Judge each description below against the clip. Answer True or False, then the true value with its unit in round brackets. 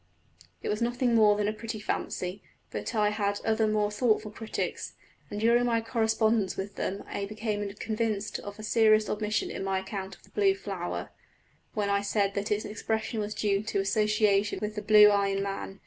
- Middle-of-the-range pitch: False (210 Hz)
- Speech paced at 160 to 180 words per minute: False (195 wpm)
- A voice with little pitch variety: True (1.5 semitones)